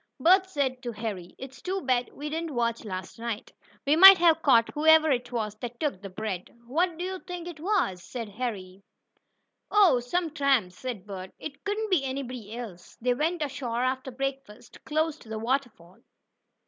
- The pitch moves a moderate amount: No, wide, 5.9 semitones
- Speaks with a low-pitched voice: No, very high, 260 Hz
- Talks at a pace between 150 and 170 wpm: No, average, 185 wpm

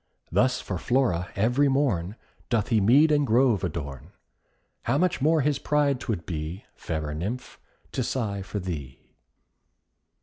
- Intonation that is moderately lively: No, wide, 7.3 semitones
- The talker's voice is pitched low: Yes, low, 110 Hz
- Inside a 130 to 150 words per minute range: Yes, average, 140 wpm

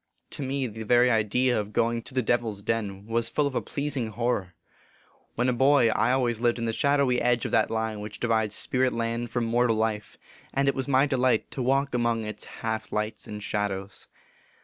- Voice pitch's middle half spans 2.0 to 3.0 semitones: Yes, average, 2.7 semitones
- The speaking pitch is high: No, low, 115 Hz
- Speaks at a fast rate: Yes, fast, 210 wpm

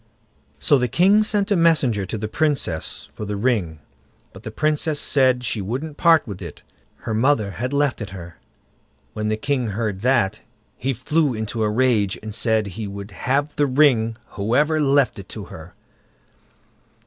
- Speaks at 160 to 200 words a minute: Yes, average, 170 wpm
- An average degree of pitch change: No, wide, 5.7 semitones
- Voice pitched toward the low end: Yes, low, 120 Hz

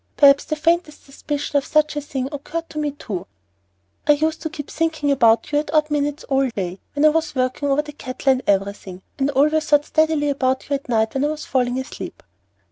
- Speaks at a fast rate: Yes, fast, 220 wpm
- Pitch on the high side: Yes, very high, 290 Hz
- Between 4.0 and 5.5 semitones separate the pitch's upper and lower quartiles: No, narrow, 2.6 semitones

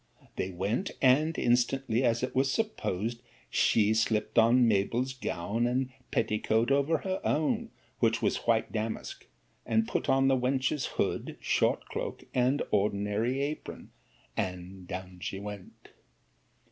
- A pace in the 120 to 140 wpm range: Yes, slow, 135 wpm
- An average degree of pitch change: Yes, average, 4.1 semitones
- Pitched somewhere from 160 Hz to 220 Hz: No, low, 115 Hz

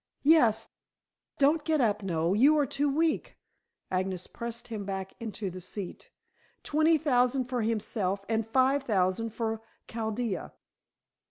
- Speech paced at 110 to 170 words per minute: Yes, slow, 135 wpm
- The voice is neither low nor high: No, high, 225 Hz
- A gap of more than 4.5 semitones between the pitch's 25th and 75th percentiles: Yes, wide, 5.6 semitones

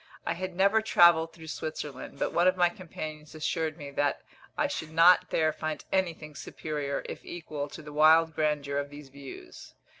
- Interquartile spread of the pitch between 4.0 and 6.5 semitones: No, narrow, 2.4 semitones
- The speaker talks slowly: No, average, 180 wpm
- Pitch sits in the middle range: Yes, medium, 155 Hz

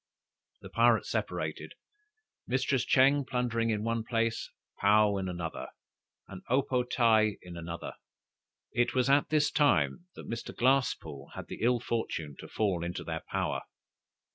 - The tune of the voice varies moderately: Yes, average, 4.2 semitones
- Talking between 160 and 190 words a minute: No, average, 150 wpm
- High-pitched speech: No, low, 115 Hz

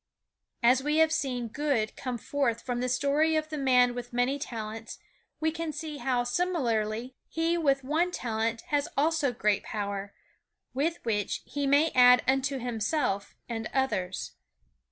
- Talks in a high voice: Yes, very high, 255 Hz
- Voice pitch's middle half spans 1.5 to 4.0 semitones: No, average, 4.5 semitones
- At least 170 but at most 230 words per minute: No, average, 155 wpm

